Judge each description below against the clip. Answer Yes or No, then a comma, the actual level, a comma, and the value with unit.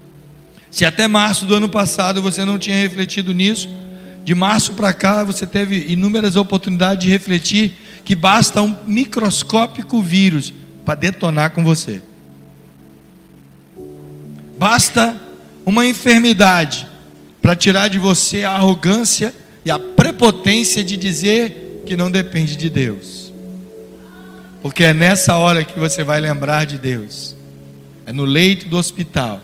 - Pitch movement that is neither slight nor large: No, wide, 5.9 semitones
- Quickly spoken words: No, average, 130 wpm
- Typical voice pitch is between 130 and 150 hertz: No, medium, 185 Hz